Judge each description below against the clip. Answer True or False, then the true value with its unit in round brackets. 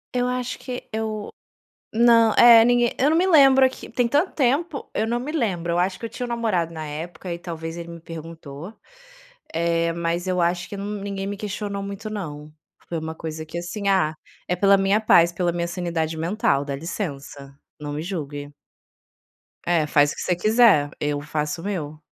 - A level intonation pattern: False (5.5 semitones)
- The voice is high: False (180 Hz)